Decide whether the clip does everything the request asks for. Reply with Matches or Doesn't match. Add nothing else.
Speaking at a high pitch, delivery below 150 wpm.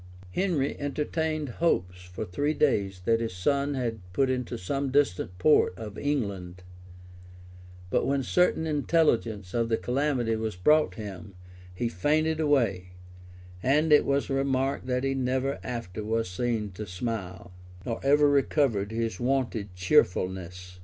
Doesn't match